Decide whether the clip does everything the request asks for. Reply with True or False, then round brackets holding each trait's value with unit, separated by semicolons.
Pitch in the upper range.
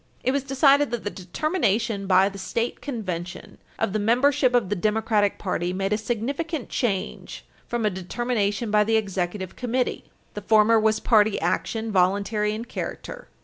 True (215 Hz)